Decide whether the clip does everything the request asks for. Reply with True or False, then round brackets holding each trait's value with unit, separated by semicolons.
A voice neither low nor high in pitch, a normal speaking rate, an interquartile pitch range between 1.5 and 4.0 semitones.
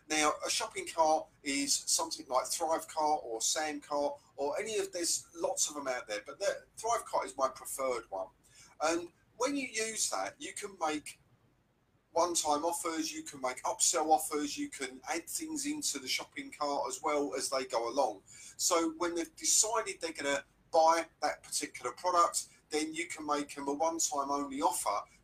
True (155 Hz; 190 wpm; 3.3 semitones)